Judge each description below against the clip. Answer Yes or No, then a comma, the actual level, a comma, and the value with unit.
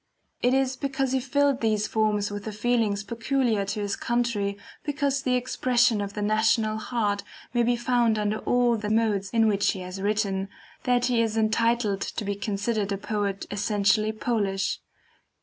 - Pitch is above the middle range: Yes, high, 220 Hz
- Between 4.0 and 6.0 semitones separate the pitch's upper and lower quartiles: No, average, 3.0 semitones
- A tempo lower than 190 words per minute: Yes, average, 170 wpm